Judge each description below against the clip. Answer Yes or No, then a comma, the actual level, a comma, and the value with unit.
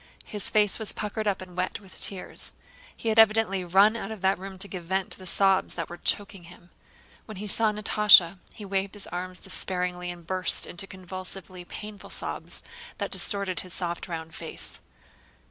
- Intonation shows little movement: Yes, narrow, 2.3 semitones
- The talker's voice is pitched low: No, high, 190 Hz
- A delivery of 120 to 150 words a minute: No, average, 185 wpm